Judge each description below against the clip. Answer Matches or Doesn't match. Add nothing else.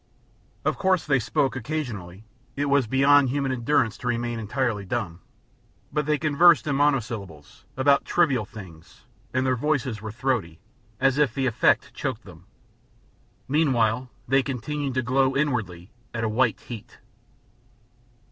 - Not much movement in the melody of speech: Doesn't match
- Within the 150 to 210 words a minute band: Doesn't match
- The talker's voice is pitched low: Matches